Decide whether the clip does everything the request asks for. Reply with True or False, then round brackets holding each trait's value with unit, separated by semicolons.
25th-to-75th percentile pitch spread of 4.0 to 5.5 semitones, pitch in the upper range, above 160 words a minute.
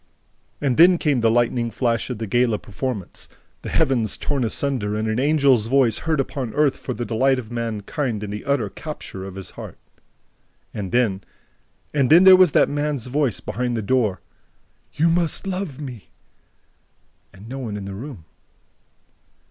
False (4.5 semitones; 125 Hz; 170 wpm)